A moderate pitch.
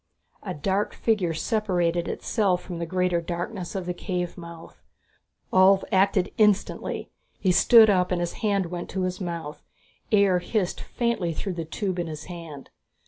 Yes: medium, 180 Hz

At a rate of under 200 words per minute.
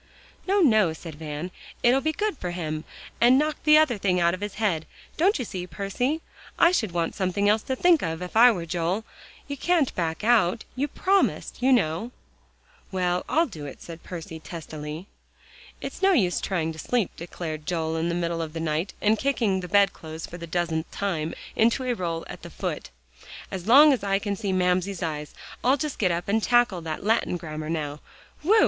No: fast, 205 wpm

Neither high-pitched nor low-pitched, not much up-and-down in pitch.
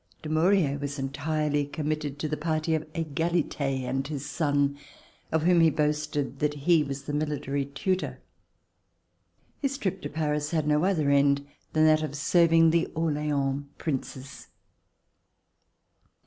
Yes: medium, 150 Hz; narrow, 2.1 semitones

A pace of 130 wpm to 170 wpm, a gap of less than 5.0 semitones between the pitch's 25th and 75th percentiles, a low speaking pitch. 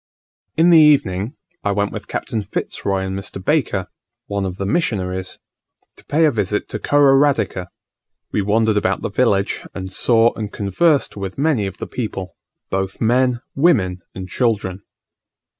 No: average, 160 wpm; average, 5.3 semitones; low, 105 Hz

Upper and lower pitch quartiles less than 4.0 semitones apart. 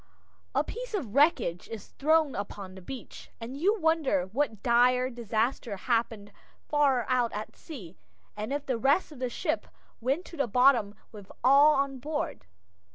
No: average, 5.0 semitones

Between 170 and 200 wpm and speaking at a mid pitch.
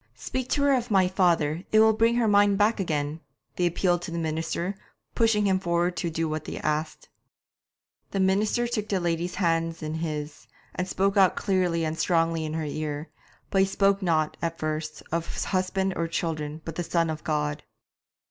Yes: average, 195 wpm; medium, 170 Hz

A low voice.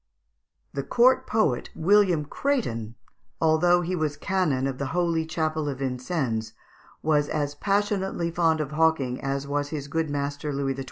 No: medium, 155 Hz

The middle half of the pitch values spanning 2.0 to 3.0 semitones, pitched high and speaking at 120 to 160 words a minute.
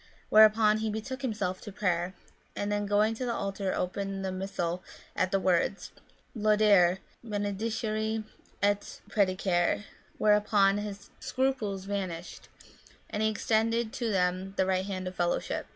Yes: narrow, 2.4 semitones; high, 205 Hz; average, 140 wpm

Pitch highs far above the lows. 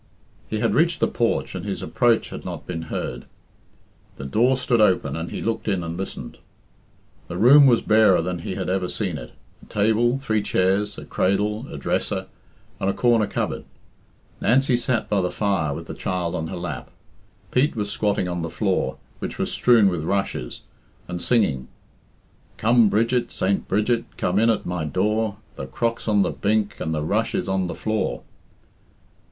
No: average, 4.0 semitones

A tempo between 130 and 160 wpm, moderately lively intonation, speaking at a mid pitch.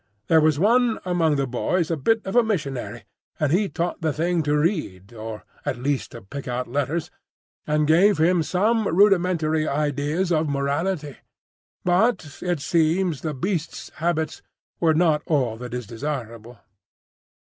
Yes: average, 155 wpm; average, 4.2 semitones; medium, 155 Hz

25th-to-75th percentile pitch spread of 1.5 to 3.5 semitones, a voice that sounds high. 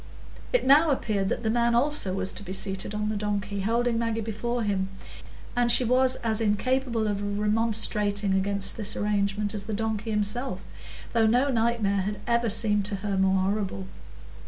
Yes: average, 2.7 semitones; high, 210 Hz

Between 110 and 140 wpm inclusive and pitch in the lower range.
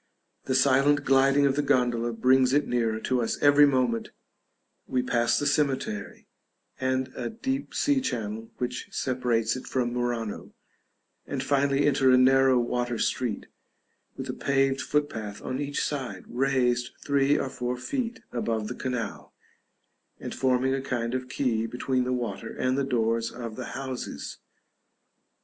No: average, 150 wpm; low, 130 Hz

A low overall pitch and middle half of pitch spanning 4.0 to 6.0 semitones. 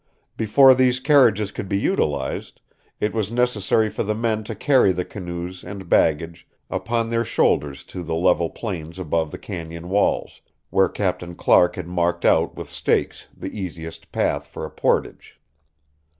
Yes: very low, 95 Hz; average, 4.6 semitones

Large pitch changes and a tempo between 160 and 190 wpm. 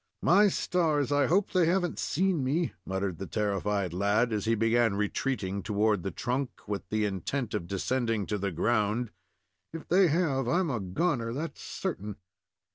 Yes: wide, 6.8 semitones; average, 170 wpm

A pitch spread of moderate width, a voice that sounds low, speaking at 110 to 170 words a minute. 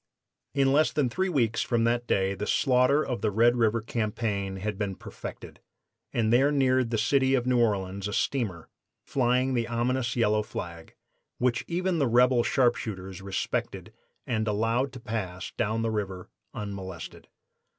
Yes: average, 3.7 semitones; low, 115 Hz; average, 160 wpm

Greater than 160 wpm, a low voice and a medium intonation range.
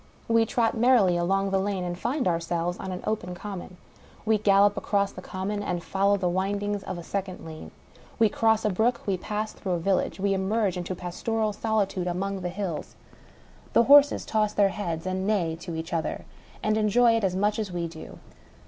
No: average, 195 wpm; high, 195 Hz; average, 3.0 semitones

